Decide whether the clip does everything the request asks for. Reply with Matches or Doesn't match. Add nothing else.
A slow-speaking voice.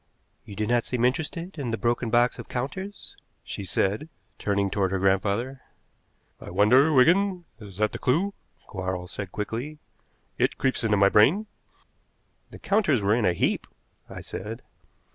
Doesn't match